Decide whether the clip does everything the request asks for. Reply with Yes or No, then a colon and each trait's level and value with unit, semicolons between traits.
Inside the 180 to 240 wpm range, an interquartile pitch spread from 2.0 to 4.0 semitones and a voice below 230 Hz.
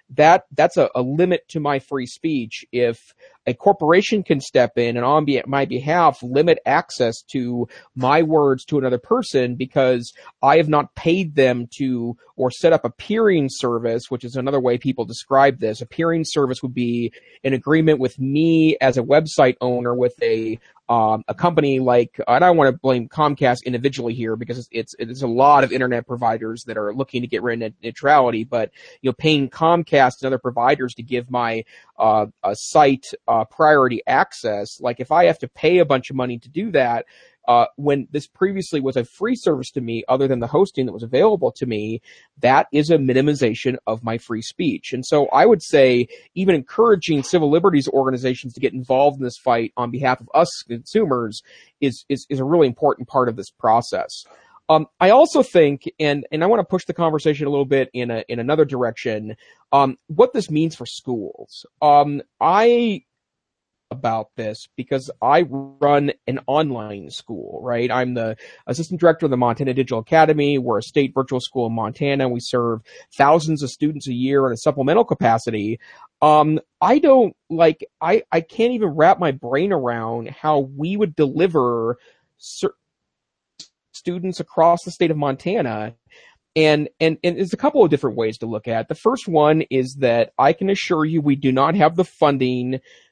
No: average, 190 wpm; average, 4.4 semitones; low, 135 Hz